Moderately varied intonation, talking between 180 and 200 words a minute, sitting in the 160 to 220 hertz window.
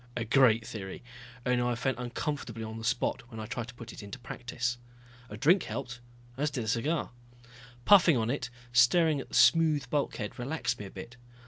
No: average, 3.6 semitones; average, 195 wpm; low, 125 Hz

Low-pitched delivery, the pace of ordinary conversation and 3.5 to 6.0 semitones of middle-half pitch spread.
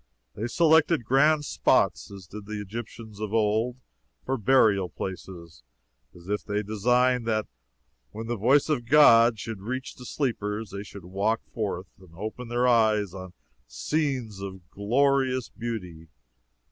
Yes: low, 110 Hz; average, 145 wpm; average, 3.9 semitones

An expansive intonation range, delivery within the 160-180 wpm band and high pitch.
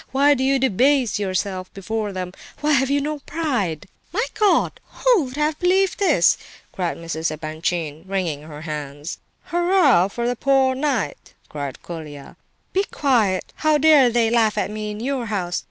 Yes: wide, 8.5 semitones; average, 170 wpm; high, 225 Hz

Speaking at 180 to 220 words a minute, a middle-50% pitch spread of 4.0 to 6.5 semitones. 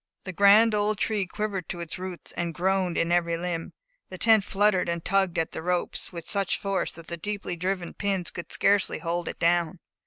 No: fast, 205 wpm; average, 2.7 semitones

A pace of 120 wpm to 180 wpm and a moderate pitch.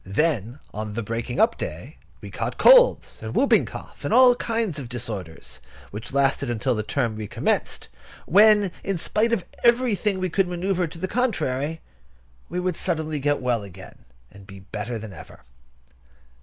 Yes: average, 165 wpm; medium, 145 Hz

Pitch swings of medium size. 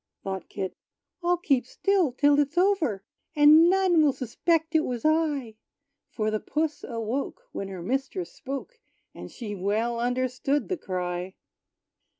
No: wide, 6.5 semitones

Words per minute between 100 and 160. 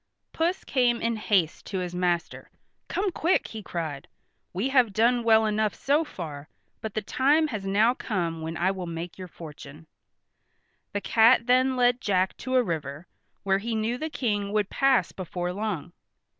No: average, 170 wpm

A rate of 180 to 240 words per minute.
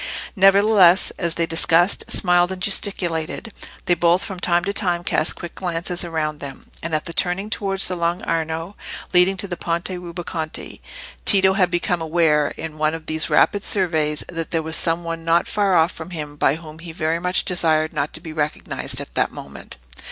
Yes: average, 190 wpm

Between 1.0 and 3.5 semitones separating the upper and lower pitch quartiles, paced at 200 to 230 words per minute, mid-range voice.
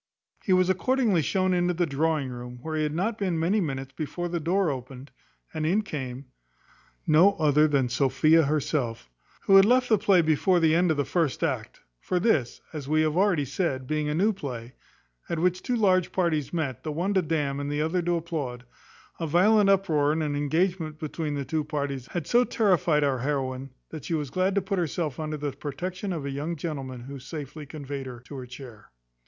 No: average, 4.3 semitones; fast, 205 wpm; medium, 155 Hz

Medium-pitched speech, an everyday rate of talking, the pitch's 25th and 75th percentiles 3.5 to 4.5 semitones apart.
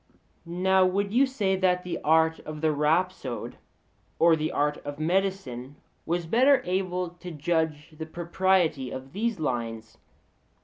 Yes: medium, 170 Hz; average, 145 wpm; average, 4.0 semitones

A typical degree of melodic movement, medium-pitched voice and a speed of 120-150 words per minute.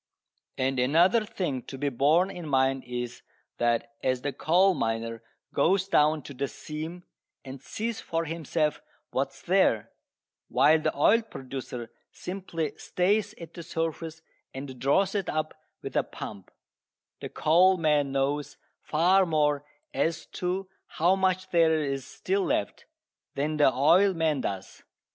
Yes: average, 4.8 semitones; medium, 155 Hz; average, 145 wpm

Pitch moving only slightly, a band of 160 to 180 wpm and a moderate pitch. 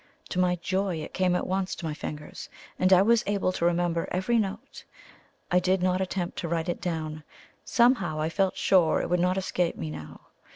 No: narrow, 2.1 semitones; fast, 205 wpm; medium, 180 Hz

